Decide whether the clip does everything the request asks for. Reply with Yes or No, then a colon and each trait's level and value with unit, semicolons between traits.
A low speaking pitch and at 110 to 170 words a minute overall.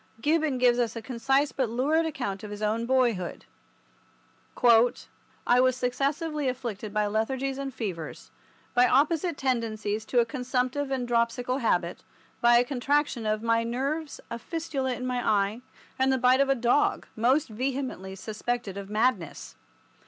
No: high, 245 Hz; average, 150 wpm